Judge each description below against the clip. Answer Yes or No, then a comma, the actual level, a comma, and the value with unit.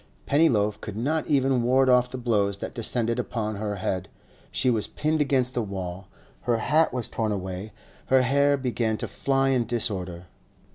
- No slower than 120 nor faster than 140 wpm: No, average, 175 wpm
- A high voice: No, low, 120 Hz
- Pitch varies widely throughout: No, average, 4.3 semitones